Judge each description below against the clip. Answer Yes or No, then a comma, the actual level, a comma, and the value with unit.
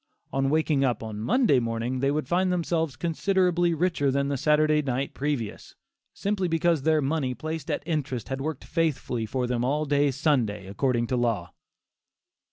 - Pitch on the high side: No, medium, 140 Hz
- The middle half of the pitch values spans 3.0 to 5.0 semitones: Yes, average, 4.2 semitones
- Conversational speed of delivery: Yes, average, 170 wpm